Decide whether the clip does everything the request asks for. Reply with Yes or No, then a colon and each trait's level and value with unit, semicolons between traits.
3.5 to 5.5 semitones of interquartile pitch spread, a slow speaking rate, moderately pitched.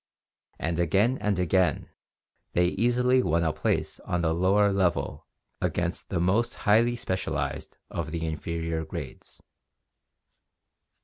No: average, 3.8 semitones; slow, 120 wpm; very low, 90 Hz